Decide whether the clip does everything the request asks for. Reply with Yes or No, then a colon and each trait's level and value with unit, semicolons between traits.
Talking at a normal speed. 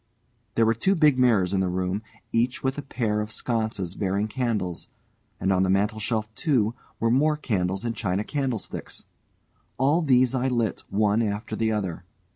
Yes: average, 170 wpm